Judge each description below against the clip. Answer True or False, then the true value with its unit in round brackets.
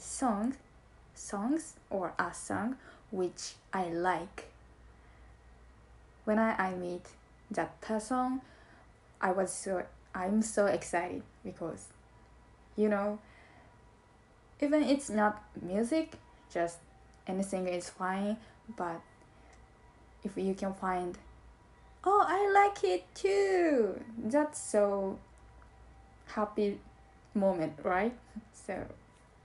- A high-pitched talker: True (210 Hz)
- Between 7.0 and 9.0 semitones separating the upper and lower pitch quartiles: False (5.1 semitones)